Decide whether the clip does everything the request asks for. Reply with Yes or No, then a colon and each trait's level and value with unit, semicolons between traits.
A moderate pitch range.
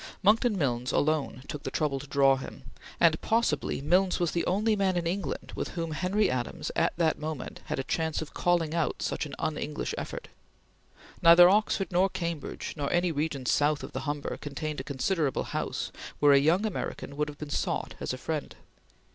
Yes: average, 3.5 semitones